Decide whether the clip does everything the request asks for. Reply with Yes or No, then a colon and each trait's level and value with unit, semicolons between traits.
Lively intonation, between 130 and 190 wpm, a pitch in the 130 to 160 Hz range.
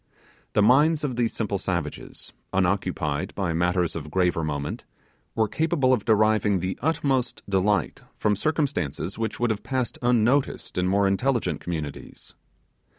No: wide, 5.7 semitones; average, 140 wpm; low, 100 Hz